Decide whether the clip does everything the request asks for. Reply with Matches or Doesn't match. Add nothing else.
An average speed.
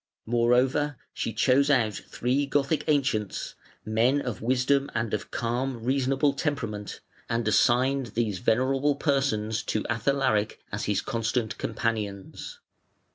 Doesn't match